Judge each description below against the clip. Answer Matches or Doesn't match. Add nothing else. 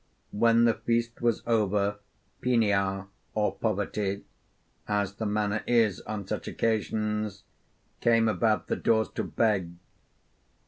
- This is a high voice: Doesn't match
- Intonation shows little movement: Matches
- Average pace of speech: Doesn't match